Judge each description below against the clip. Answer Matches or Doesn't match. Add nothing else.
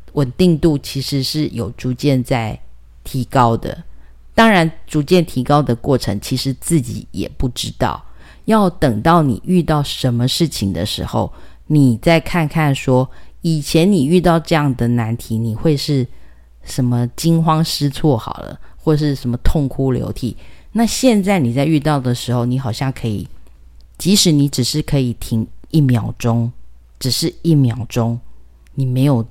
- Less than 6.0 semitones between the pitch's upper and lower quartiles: Matches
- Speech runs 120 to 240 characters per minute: Matches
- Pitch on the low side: Matches